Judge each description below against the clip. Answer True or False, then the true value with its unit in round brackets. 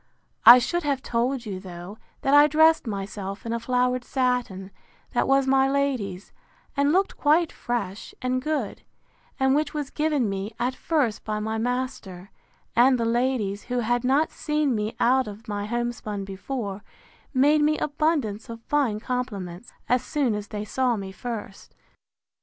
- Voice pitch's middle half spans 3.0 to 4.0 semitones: False (4.5 semitones)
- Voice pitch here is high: True (245 Hz)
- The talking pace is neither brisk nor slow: True (160 wpm)